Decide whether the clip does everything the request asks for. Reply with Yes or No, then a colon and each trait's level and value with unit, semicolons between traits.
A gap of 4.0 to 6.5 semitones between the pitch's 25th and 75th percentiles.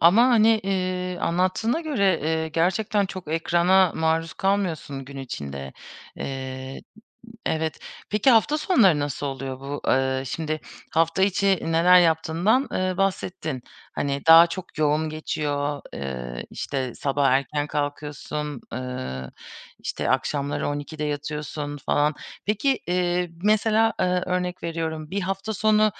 Yes: average, 4.7 semitones